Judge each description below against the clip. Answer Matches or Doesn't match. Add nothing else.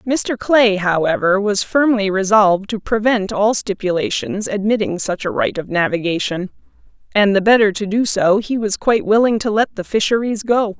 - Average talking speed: Matches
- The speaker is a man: Doesn't match